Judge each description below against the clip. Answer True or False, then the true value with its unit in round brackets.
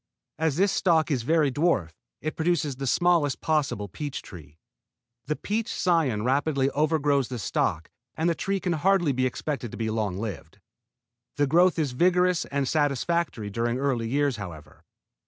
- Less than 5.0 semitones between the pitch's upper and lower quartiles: False (5.6 semitones)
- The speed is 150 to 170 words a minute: True (165 wpm)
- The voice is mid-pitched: True (145 Hz)